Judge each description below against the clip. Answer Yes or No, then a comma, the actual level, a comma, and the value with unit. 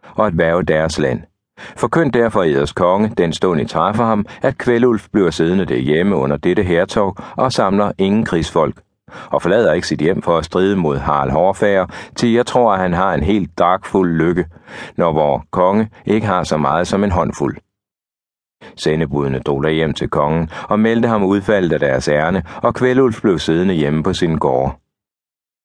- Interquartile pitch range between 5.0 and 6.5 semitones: Yes, wide, 5.6 semitones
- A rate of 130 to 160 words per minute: No, average, 180 wpm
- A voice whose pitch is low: Yes, very low, 95 Hz